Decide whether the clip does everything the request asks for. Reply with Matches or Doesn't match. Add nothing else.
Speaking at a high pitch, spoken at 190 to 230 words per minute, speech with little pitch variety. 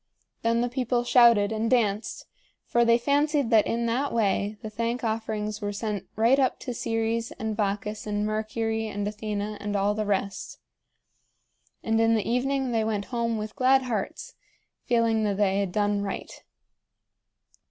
Doesn't match